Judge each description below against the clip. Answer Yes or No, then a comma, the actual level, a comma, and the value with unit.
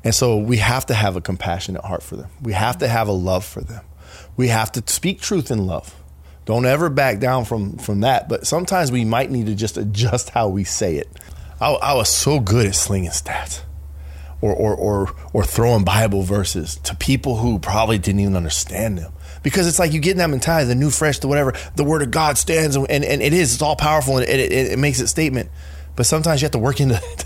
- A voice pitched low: Yes, low, 115 Hz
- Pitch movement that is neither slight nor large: No, wide, 6.8 semitones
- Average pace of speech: No, fast, 240 wpm